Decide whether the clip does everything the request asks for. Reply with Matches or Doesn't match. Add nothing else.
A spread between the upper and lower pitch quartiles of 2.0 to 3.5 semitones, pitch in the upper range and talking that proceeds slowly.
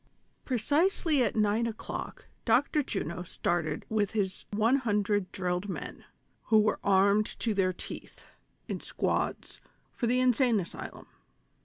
Doesn't match